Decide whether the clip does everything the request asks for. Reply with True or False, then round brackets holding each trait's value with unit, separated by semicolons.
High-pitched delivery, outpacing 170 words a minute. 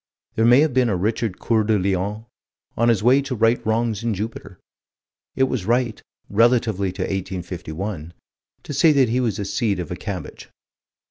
False (110 Hz; 180 wpm)